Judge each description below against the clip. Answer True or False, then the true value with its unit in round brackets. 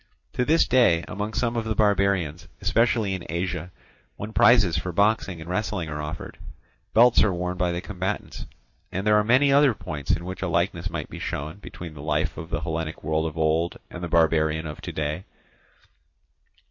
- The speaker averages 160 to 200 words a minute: True (190 wpm)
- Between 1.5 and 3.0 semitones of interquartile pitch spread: False (4.7 semitones)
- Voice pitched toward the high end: False (90 Hz)